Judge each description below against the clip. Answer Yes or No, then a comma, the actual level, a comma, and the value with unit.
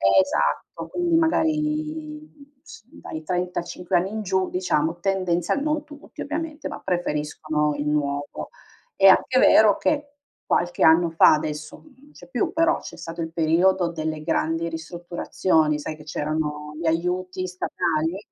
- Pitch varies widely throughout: Yes, wide, 8.4 semitones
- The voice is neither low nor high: Yes, medium, 175 Hz